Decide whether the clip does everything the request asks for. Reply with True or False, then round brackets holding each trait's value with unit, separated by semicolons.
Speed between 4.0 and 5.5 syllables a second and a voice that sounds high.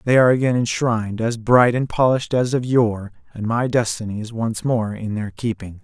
False (5.3 syllables/s; 115 Hz)